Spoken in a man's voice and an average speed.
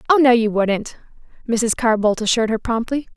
No: female; average, 190 wpm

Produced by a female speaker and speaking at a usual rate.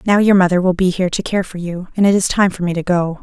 No: female; fast, 335 wpm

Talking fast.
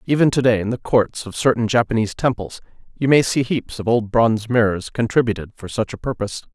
Yes: fast, 210 wpm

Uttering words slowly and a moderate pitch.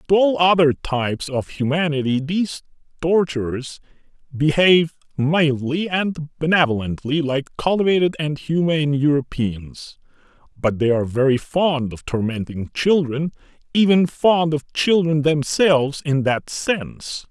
Yes: slow, 115 wpm; medium, 150 Hz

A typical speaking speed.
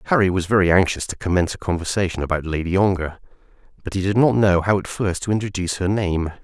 No: fast, 215 wpm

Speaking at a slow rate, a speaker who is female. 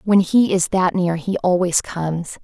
No: average, 200 wpm; female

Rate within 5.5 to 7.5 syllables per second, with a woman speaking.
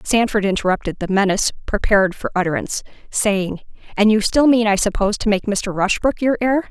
Yes: 5.9 syllables/s; female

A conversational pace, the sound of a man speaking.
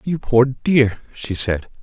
Yes: average, 165 wpm; male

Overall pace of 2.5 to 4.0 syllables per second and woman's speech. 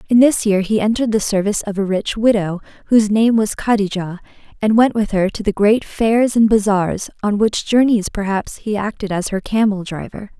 No: 5.3 syllables/s; female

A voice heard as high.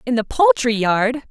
Yes: high, 245 Hz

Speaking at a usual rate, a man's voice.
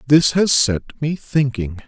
Yes: average, 160 wpm; male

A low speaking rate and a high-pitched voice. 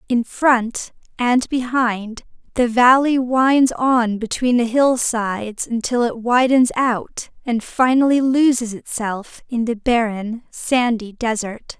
Yes: slow, 125 wpm; high, 240 Hz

